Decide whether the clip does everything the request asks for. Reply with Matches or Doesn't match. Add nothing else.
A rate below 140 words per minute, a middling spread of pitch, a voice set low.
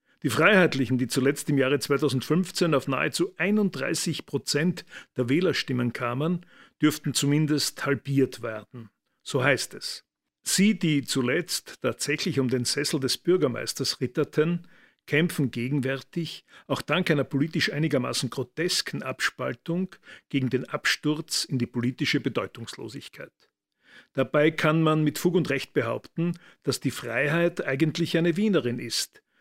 Doesn't match